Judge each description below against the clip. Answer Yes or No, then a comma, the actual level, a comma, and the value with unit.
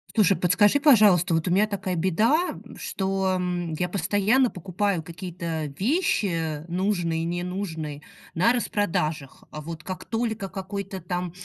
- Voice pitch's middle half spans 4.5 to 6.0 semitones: No, average, 3.4 semitones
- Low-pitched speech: No, medium, 185 Hz